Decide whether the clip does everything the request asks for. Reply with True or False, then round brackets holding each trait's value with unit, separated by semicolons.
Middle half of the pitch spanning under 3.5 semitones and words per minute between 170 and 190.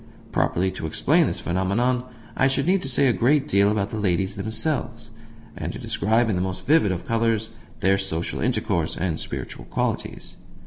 False (4.8 semitones; 180 wpm)